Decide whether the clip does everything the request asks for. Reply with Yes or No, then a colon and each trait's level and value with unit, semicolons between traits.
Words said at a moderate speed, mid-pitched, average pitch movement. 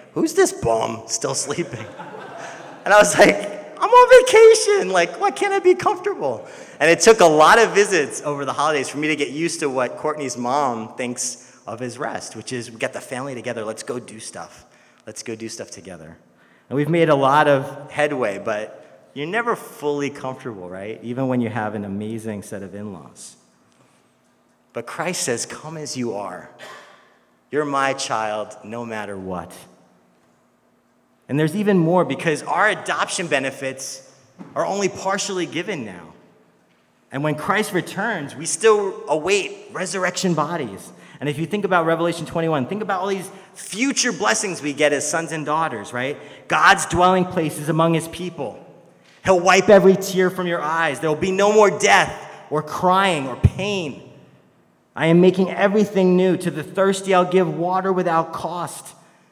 No: average, 170 wpm; medium, 155 Hz; wide, 7.3 semitones